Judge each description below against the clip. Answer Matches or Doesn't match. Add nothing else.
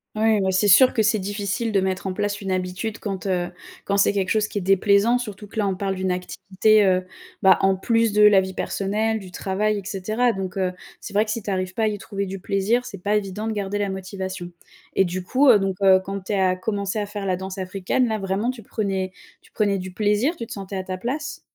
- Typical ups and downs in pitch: Doesn't match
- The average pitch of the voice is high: Matches